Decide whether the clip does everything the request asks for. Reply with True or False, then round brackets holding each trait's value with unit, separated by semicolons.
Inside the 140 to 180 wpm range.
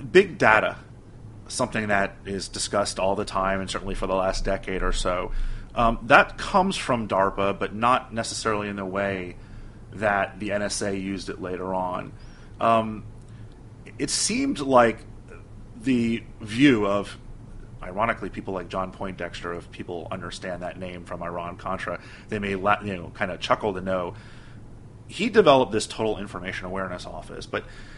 True (155 wpm)